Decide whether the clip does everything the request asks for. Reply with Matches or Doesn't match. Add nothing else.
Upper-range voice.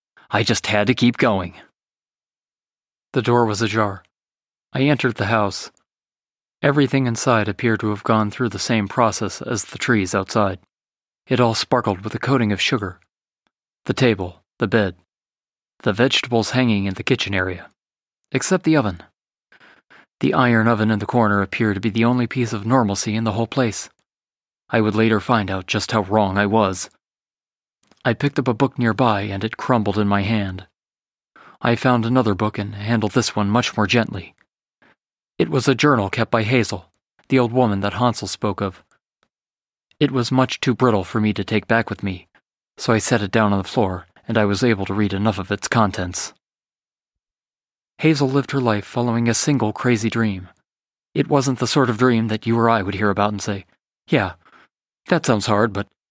Doesn't match